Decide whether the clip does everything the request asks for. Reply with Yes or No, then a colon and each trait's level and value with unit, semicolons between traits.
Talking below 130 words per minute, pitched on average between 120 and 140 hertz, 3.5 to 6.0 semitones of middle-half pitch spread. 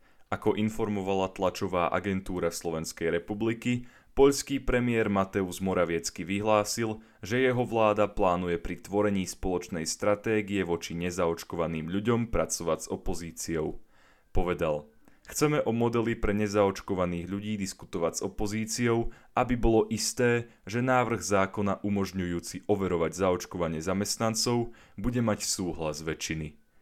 No: slow, 110 wpm; low, 100 Hz; average, 4.0 semitones